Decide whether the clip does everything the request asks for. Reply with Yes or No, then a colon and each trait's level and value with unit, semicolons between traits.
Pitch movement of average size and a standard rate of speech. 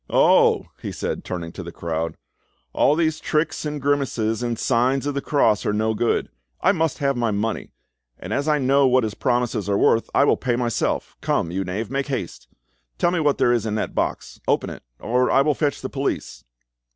No: average, 4.7 semitones; fast, 210 wpm